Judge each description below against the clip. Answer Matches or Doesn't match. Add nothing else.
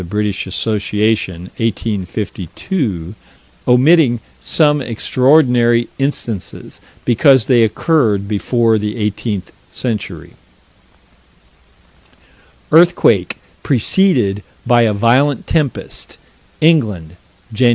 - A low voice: Matches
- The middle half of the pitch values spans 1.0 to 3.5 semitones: Doesn't match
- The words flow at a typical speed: Doesn't match